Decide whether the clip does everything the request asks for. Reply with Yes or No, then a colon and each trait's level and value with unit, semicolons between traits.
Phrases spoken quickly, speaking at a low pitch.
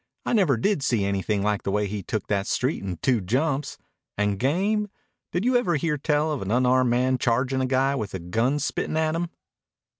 Yes: fast, 210 wpm; low, 130 Hz